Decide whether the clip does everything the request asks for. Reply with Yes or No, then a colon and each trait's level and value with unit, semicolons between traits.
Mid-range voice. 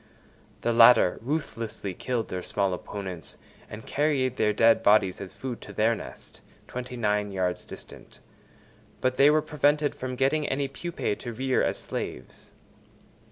No: low, 120 Hz